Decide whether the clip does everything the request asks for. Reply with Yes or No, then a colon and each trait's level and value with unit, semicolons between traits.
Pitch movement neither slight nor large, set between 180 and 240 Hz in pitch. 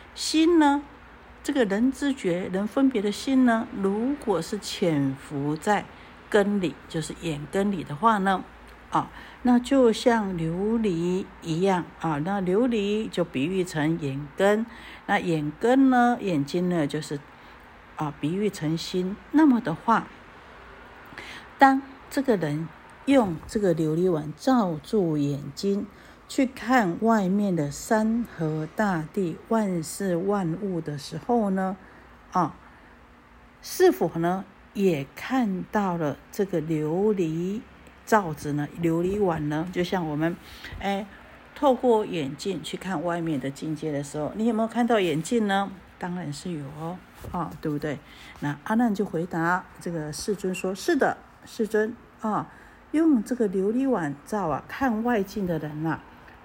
No: wide, 5.7 semitones; high, 190 Hz